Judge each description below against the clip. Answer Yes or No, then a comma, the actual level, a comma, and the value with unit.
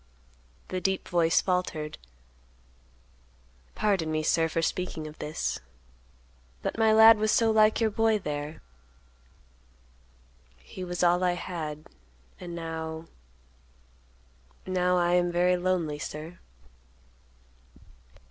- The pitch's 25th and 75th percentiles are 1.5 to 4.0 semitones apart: Yes, average, 3.4 semitones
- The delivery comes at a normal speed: No, slow, 100 wpm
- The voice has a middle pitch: Yes, medium, 170 Hz